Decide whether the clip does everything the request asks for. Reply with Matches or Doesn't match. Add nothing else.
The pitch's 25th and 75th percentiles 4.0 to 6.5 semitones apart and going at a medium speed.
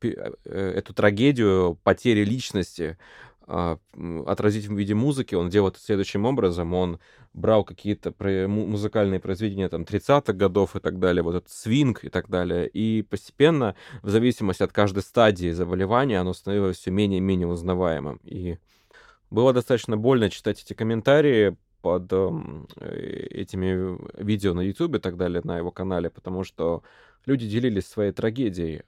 Doesn't match